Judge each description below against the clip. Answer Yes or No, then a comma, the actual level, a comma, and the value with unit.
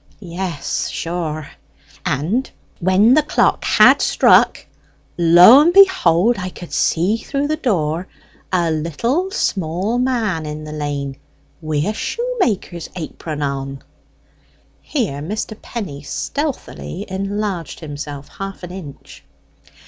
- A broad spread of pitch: Yes, wide, 6.7 semitones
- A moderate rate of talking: No, slow, 115 wpm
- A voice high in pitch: No, medium, 180 Hz